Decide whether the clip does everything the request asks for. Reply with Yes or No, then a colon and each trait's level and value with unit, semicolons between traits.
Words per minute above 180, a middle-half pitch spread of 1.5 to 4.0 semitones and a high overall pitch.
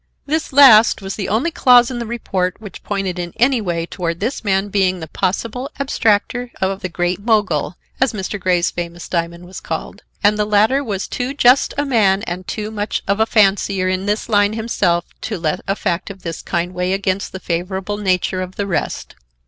Yes: average, 200 wpm; average, 3.4 semitones; high, 195 Hz